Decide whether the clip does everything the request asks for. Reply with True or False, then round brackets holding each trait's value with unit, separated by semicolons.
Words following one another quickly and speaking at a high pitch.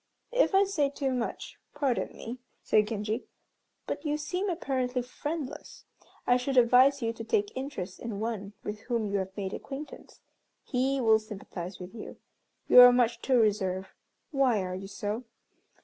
False (165 wpm; 245 Hz)